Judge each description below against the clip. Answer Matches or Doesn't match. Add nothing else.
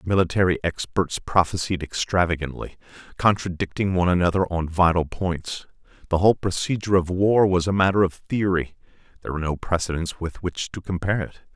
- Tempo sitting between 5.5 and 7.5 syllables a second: Matches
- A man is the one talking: Matches